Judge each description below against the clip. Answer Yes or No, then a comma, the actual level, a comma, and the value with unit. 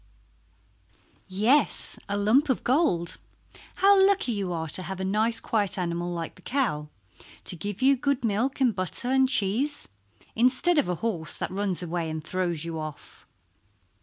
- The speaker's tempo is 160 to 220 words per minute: Yes, average, 165 wpm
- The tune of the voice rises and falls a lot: Yes, wide, 6.9 semitones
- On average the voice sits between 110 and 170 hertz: No, high, 205 Hz